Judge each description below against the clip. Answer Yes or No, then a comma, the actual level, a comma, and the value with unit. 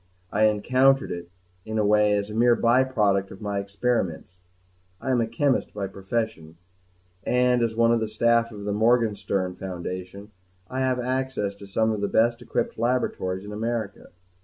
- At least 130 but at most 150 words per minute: No, average, 170 wpm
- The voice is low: Yes, low, 110 Hz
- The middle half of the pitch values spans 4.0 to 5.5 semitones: No, average, 3.1 semitones